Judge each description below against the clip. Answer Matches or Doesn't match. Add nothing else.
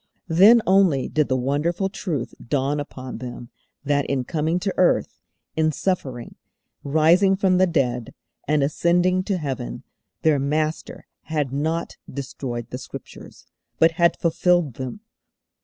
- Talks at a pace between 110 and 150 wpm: Matches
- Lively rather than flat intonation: Doesn't match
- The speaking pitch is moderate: Matches